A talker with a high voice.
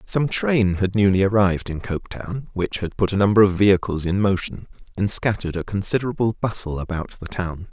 No: low, 100 Hz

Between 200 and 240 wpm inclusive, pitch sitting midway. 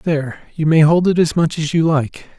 No: fast, 250 wpm; medium, 155 Hz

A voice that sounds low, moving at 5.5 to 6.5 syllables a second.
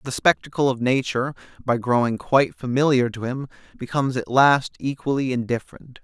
Yes: low, 130 Hz; 5.7 syllables/s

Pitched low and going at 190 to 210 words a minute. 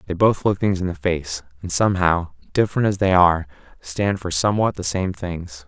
Yes: very low, 90 Hz; average, 200 wpm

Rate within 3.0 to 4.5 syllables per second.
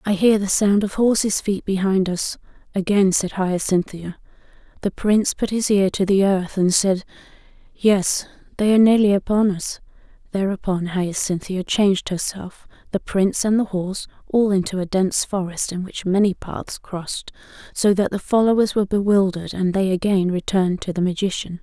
No: 5.1 syllables/s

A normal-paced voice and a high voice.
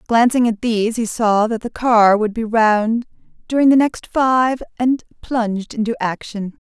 Yes: average, 170 wpm; high, 230 Hz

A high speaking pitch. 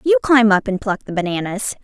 Yes: high, 220 Hz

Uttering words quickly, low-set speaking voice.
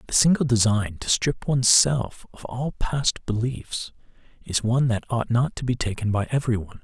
No: average, 195 wpm; low, 120 Hz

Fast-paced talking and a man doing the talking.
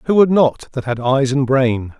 Yes: fast, 240 wpm; male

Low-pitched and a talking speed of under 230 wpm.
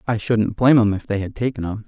No: low, 110 Hz; fast, 290 wpm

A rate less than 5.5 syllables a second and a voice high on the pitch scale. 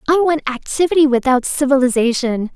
No: 5.7 syllables/s; very high, 270 Hz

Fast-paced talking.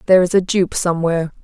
Yes: fast, 210 wpm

